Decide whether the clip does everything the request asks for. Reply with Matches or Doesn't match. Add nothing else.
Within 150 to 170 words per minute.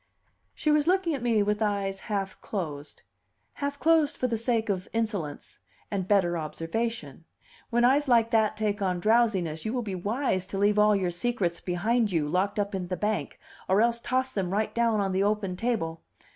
Doesn't match